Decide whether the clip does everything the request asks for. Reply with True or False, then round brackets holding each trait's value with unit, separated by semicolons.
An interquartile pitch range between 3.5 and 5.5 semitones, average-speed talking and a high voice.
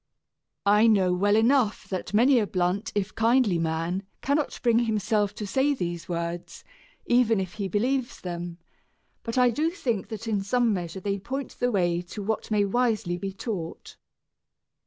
True (4.7 semitones; 165 wpm; 210 Hz)